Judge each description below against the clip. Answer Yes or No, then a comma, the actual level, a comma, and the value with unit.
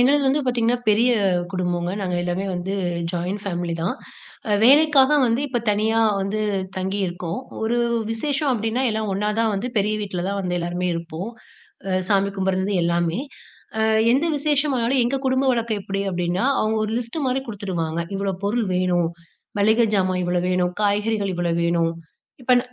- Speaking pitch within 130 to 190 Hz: No, high, 200 Hz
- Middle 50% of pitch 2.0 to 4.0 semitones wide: No, average, 4.7 semitones